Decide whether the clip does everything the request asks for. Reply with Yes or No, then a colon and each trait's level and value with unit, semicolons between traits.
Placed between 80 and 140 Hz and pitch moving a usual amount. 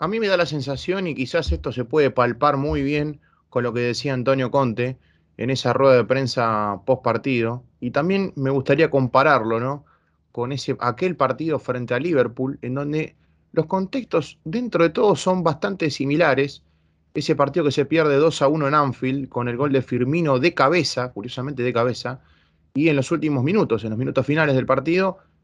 Yes: low, 135 Hz; average, 4.0 semitones